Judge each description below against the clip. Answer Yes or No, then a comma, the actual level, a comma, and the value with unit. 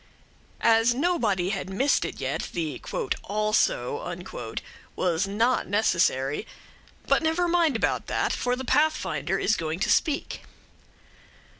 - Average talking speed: No, slow, 120 wpm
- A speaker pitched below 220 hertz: No, high, 225 Hz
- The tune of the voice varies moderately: No, wide, 8.0 semitones